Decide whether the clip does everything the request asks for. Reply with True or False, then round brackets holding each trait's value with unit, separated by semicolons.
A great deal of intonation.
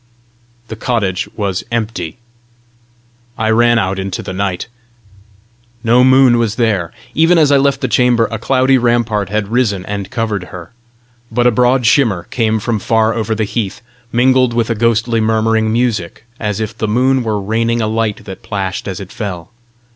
False (2.7 semitones)